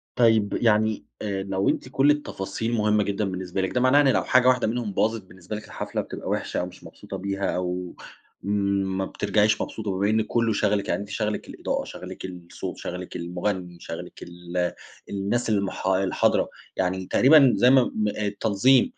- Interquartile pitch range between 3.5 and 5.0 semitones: No, average, 3.0 semitones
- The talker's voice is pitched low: Yes, low, 100 Hz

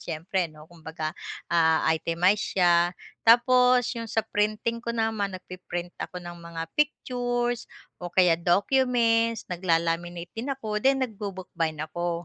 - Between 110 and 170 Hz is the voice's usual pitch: No, medium, 185 Hz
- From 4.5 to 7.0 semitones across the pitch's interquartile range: Yes, average, 5.2 semitones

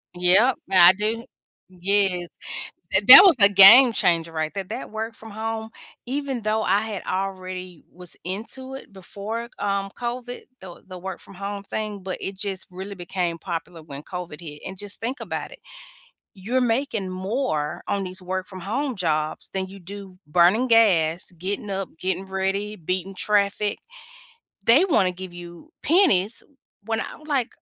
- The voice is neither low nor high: No, high, 195 Hz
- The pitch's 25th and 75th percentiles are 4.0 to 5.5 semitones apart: No, average, 3.4 semitones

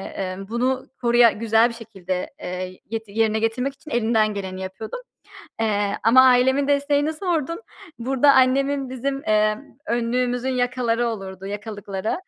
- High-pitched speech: Yes, high, 230 Hz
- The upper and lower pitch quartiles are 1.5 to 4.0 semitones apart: Yes, average, 3.7 semitones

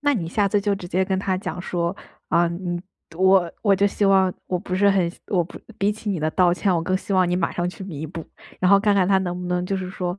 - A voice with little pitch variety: Yes, narrow, 2.0 semitones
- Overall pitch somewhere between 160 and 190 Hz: Yes, medium, 185 Hz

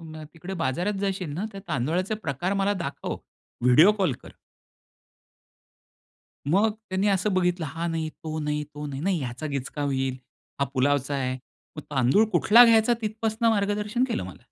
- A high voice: No, medium, 170 Hz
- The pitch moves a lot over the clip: Yes, wide, 6.1 semitones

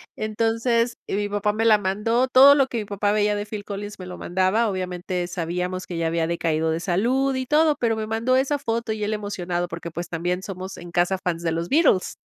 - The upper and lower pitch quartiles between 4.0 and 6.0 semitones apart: Yes, average, 4.3 semitones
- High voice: Yes, high, 205 Hz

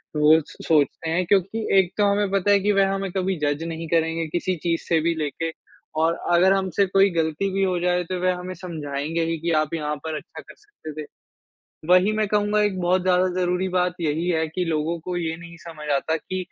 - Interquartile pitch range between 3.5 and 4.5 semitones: No, average, 2.7 semitones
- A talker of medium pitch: Yes, medium, 175 Hz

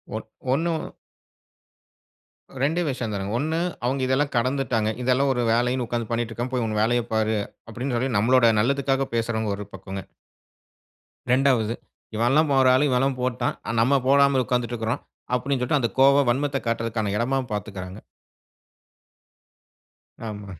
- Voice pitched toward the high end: No, low, 125 Hz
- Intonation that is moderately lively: Yes, average, 3.2 semitones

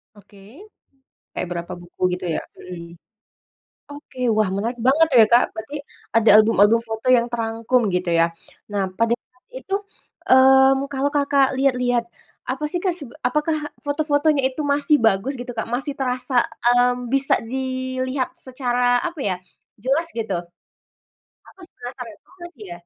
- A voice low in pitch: No, very high, 250 Hz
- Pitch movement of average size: Yes, average, 3.7 semitones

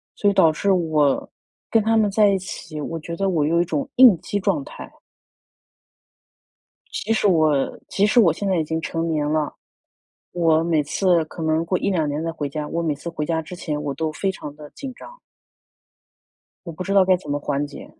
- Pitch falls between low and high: Yes, medium, 165 Hz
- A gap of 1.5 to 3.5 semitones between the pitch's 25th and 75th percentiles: No, average, 4.0 semitones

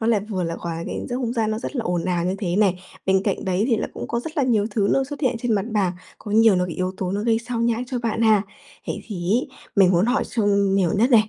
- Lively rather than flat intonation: No, average, 3.6 semitones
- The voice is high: Yes, high, 215 Hz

